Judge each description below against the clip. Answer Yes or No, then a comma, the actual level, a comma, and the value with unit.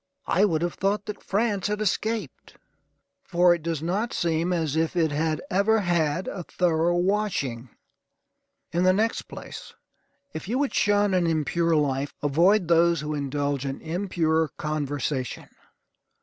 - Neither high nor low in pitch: Yes, medium, 170 Hz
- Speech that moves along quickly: No, average, 150 wpm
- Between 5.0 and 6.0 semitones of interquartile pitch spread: No, average, 4.3 semitones